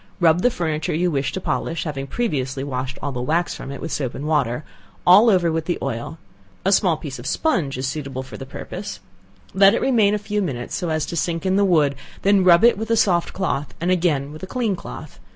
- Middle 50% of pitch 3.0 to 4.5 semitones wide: No, wide, 5.5 semitones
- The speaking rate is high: Yes, fast, 240 wpm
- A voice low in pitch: No, medium, 165 Hz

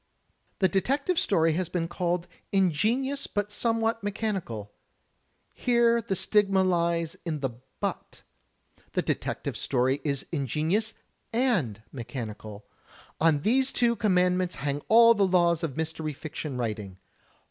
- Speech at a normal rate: No, slow, 125 wpm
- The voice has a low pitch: No, medium, 175 Hz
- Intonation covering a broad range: Yes, wide, 6.8 semitones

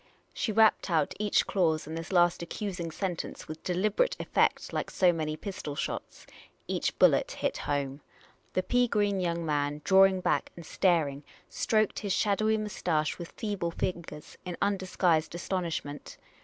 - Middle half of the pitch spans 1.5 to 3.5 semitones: No, average, 4.0 semitones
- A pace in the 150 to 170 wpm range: Yes, average, 155 wpm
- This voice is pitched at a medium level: Yes, medium, 175 Hz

